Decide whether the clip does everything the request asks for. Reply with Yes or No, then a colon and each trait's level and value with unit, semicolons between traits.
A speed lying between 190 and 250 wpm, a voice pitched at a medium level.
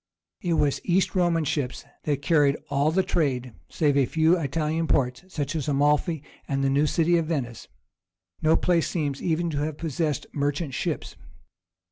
No: average, 165 wpm; medium, 150 Hz